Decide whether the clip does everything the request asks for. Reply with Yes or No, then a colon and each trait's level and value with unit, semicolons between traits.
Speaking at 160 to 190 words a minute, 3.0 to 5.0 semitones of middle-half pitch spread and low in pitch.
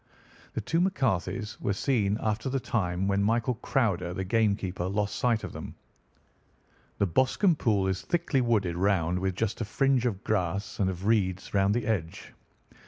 Yes: average, 170 wpm; average, 3.9 semitones; low, 105 Hz